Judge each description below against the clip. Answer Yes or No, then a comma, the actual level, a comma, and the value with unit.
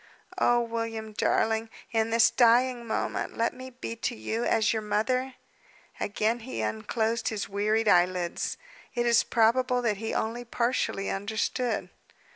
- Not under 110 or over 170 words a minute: Yes, average, 140 wpm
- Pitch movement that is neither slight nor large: No, narrow, 1.9 semitones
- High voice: Yes, high, 225 Hz